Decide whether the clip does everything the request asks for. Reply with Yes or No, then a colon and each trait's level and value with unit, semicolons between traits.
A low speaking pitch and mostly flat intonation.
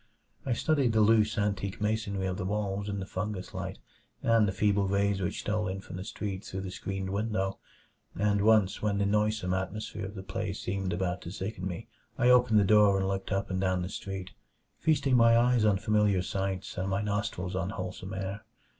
Yes: low, 100 Hz; narrow, 2.0 semitones